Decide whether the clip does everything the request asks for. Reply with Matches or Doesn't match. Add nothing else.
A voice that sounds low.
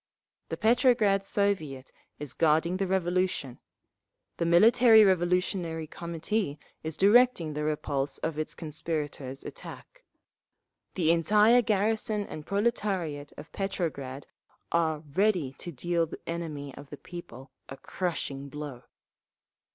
Doesn't match